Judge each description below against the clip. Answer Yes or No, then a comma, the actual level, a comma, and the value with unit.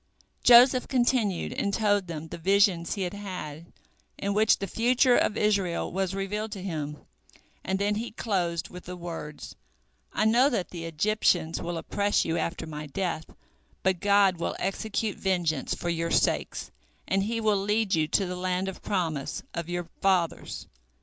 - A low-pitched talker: No, high, 190 Hz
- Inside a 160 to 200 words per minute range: Yes, average, 170 wpm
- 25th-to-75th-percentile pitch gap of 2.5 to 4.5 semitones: Yes, average, 3.5 semitones